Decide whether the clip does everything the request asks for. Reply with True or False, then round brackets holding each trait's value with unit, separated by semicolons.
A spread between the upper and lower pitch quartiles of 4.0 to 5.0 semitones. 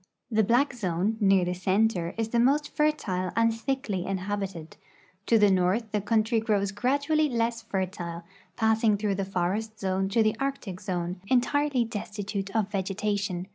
False (3.3 semitones)